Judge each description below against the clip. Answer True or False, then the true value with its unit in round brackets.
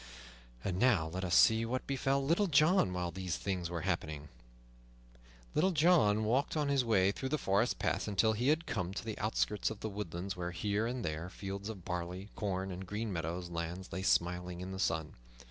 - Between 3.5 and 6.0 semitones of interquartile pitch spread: True (4.5 semitones)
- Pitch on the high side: False (100 Hz)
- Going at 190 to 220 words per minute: True (195 wpm)